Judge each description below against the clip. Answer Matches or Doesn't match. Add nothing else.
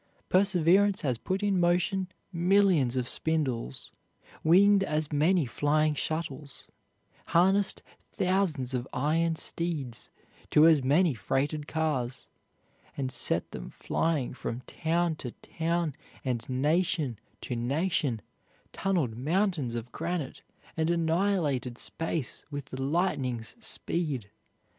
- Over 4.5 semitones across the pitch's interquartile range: Matches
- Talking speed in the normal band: Doesn't match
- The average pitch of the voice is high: Doesn't match